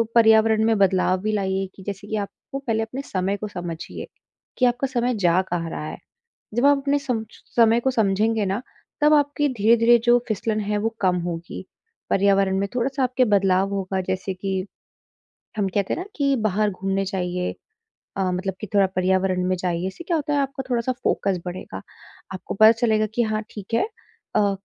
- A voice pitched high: Yes, high, 210 Hz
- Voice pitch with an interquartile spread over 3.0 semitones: Yes, average, 4.0 semitones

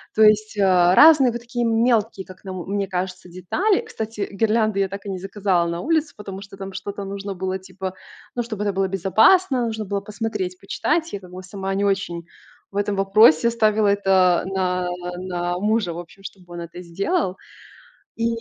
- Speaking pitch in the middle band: No, high, 195 Hz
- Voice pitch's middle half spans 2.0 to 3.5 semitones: Yes, average, 2.8 semitones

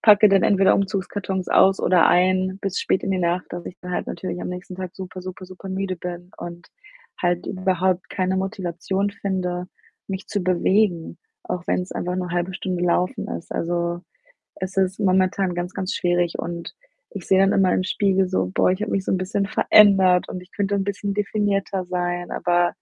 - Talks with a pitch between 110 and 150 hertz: No, medium, 185 Hz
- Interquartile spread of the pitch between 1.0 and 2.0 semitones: Yes, narrow, 1.5 semitones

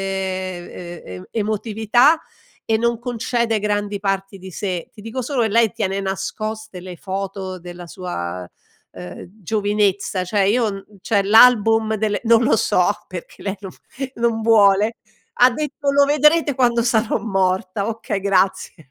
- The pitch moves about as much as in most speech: Yes, average, 3.2 semitones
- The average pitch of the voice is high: Yes, high, 205 Hz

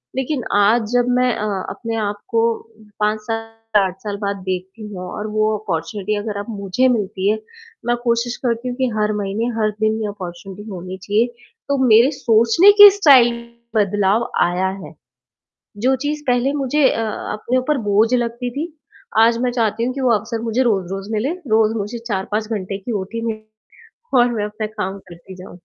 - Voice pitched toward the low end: No, high, 220 Hz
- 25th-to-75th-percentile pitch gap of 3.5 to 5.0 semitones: No, average, 3.1 semitones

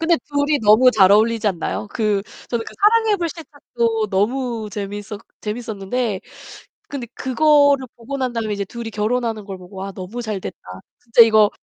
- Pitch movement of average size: Yes, average, 3.9 semitones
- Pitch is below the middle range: No, high, 225 Hz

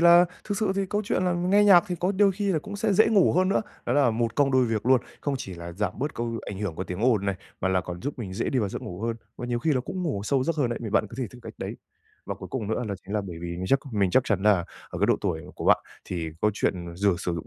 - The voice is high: No, low, 120 Hz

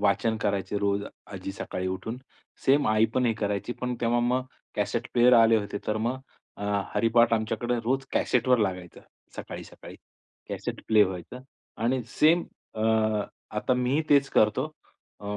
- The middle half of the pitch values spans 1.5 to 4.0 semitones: Yes, average, 3.4 semitones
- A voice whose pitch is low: Yes, low, 115 Hz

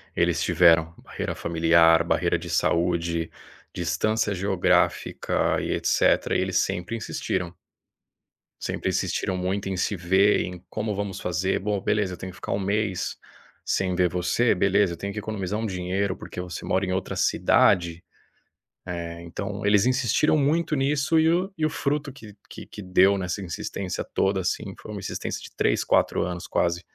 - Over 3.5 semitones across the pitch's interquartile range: No, average, 3.0 semitones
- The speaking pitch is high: No, very low, 95 Hz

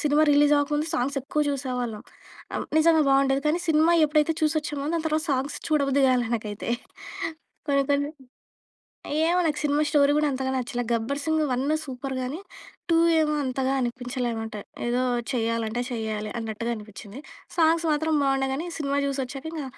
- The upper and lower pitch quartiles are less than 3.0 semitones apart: No, average, 3.5 semitones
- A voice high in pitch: Yes, very high, 275 Hz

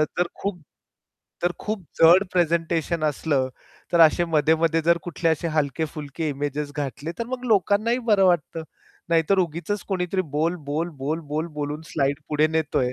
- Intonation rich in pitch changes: No, average, 2.8 semitones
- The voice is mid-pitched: Yes, medium, 165 Hz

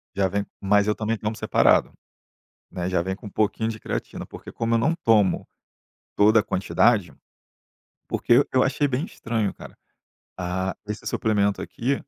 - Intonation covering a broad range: No, narrow, 2.6 semitones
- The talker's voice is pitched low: Yes, low, 105 Hz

